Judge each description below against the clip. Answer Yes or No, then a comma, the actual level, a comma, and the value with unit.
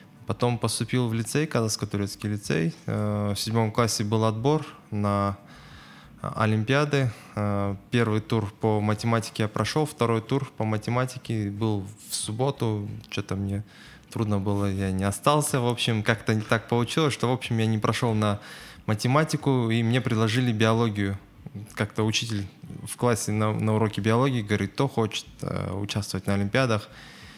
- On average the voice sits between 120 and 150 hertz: No, low, 110 Hz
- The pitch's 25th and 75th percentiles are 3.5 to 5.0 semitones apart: No, average, 2.8 semitones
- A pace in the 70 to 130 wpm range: No, average, 140 wpm